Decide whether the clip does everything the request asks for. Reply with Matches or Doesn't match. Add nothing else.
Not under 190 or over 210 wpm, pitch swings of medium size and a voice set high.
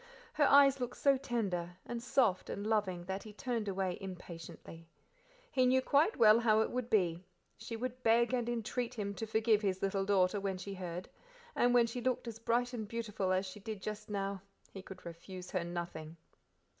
Matches